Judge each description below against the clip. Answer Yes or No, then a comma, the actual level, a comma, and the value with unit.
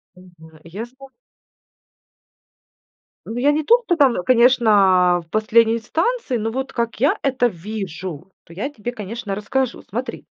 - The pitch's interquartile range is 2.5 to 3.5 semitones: No, average, 5.3 semitones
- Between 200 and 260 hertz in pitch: Yes, high, 225 Hz